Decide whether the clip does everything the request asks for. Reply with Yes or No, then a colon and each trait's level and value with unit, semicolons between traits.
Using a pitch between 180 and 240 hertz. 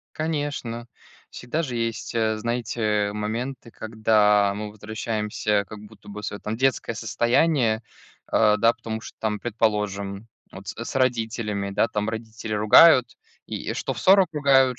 No: low, 110 Hz